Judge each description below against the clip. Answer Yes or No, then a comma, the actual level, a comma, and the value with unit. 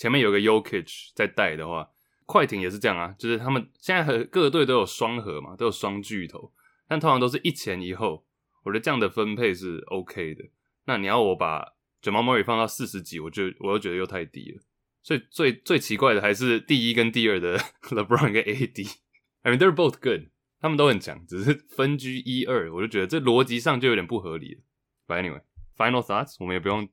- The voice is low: Yes, low, 115 Hz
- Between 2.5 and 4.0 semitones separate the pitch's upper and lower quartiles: No, average, 5.3 semitones